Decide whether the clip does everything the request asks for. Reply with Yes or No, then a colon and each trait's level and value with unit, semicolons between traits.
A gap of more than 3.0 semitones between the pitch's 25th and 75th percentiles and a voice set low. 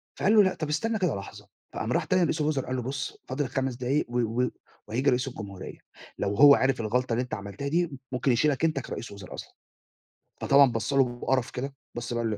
Yes: average, 3.5 semitones; low, 130 Hz